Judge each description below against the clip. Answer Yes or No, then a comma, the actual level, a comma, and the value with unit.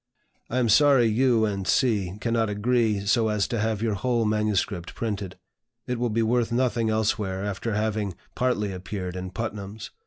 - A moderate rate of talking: Yes, average, 165 wpm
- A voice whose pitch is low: Yes, low, 110 Hz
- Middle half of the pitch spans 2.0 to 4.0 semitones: Yes, narrow, 2.5 semitones